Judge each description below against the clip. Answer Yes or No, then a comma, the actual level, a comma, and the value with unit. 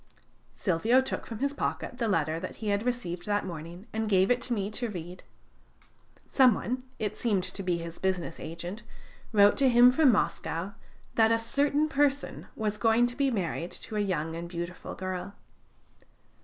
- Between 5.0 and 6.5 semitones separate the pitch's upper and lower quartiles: Yes, wide, 5.4 semitones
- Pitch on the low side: No, high, 210 Hz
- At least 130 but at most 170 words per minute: No, average, 180 wpm